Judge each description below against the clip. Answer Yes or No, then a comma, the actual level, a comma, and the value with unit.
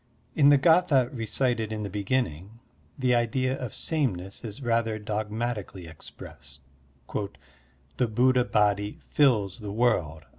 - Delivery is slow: Yes, slow, 120 wpm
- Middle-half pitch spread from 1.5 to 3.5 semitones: No, average, 4.0 semitones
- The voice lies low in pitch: Yes, low, 115 Hz